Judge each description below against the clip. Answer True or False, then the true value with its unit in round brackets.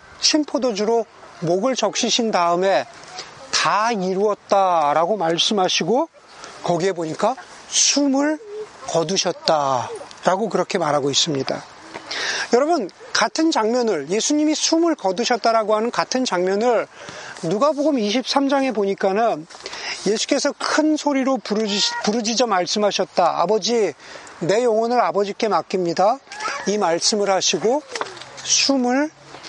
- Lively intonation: True (5.7 semitones)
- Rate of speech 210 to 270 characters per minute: True (260 characters per minute)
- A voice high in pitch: True (220 Hz)